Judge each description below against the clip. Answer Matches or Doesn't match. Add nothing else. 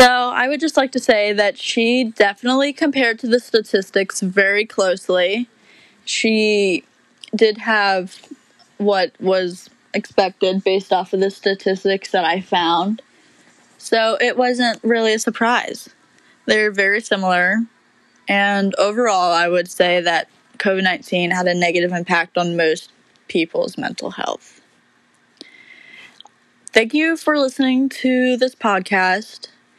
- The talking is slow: Matches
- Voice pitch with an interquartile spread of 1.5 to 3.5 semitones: Doesn't match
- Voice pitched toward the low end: Doesn't match